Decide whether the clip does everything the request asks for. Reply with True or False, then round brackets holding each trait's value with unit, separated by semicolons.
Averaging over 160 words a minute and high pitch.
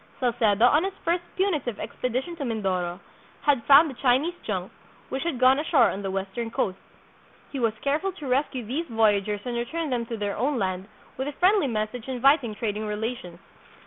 True (185 wpm; 245 Hz)